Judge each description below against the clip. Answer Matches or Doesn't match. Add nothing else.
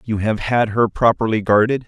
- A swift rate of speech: Doesn't match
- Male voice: Matches